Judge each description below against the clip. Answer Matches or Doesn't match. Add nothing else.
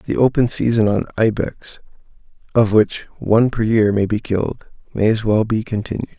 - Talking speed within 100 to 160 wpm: Doesn't match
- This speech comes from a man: Matches